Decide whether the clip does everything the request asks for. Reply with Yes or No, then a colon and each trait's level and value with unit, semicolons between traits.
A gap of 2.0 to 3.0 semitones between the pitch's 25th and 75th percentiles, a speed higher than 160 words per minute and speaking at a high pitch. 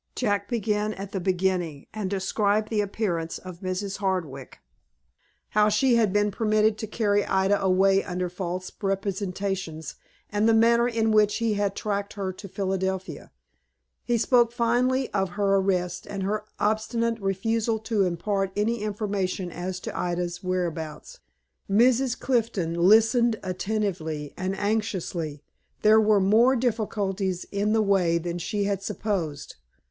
No: average, 2.7 semitones; average, 140 wpm; high, 200 Hz